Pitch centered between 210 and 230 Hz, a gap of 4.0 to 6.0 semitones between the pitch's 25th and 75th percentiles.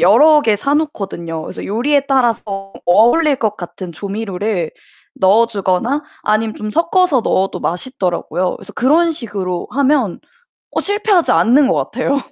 No: high, 225 Hz; wide, 6.6 semitones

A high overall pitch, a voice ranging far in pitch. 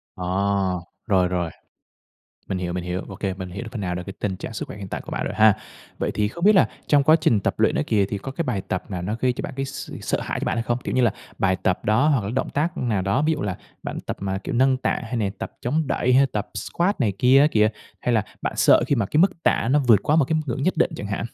No: low, 110 Hz; wide, 5.8 semitones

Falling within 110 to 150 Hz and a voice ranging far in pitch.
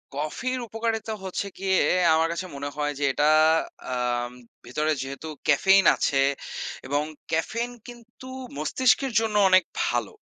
No: medium, 185 Hz; wide, 7.3 semitones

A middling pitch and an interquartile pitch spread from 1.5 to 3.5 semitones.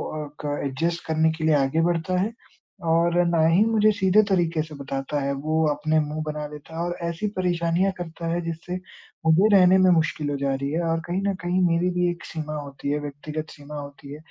Yes: medium, 160 Hz; average, 2.8 semitones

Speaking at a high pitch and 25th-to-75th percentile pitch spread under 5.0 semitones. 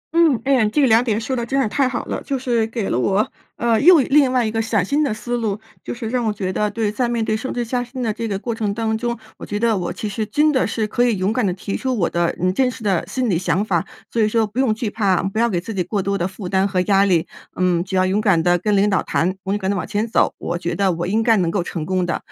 Yes: high, 215 Hz; average, 3.8 semitones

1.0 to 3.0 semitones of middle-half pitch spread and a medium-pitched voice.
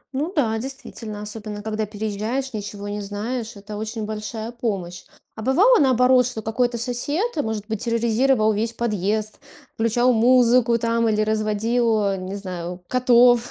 No: average, 2.7 semitones; high, 225 Hz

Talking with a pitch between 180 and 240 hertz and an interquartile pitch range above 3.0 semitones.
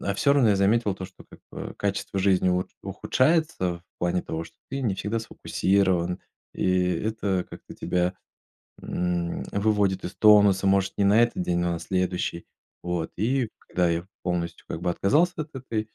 No: very low, 95 Hz; average, 3.5 semitones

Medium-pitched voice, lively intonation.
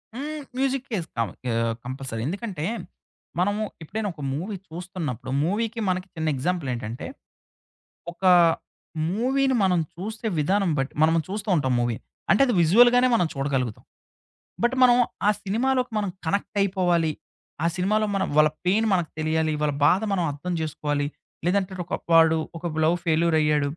Yes: medium, 180 Hz; wide, 5.7 semitones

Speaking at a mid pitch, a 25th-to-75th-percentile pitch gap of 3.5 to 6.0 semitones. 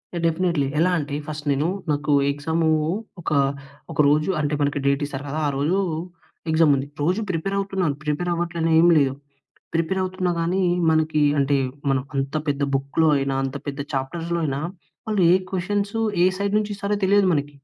Yes: medium, 160 Hz; average, 4.2 semitones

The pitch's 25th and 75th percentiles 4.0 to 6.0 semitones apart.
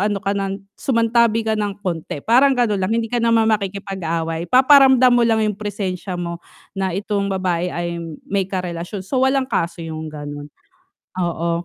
Yes: average, 4.7 semitones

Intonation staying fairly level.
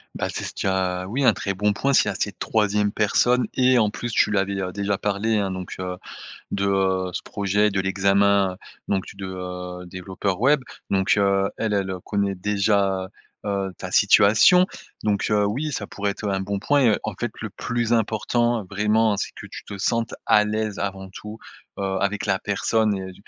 Yes: narrow, 2.1 semitones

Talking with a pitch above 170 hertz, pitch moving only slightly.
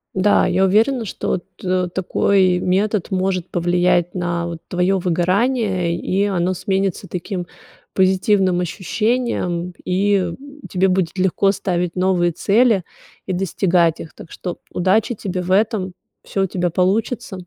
Yes: medium, 185 Hz; narrow, 1.8 semitones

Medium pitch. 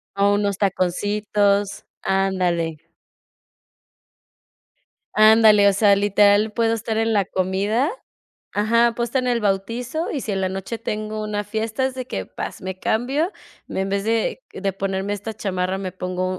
No: high, 205 Hz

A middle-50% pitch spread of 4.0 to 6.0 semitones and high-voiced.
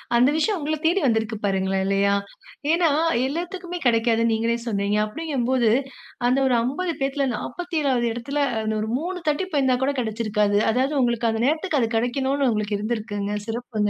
Yes: average, 4.9 semitones; high, 240 Hz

